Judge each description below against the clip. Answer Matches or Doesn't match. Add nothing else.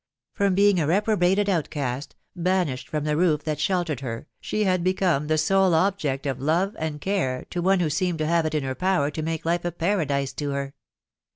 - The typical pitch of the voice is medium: Matches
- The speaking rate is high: Matches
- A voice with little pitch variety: Doesn't match